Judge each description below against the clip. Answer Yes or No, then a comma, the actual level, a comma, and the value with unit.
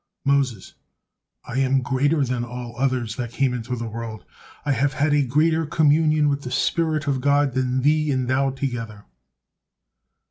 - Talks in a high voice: No, low, 135 Hz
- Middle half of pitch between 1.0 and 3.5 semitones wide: Yes, average, 2.8 semitones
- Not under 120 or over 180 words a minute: Yes, average, 165 wpm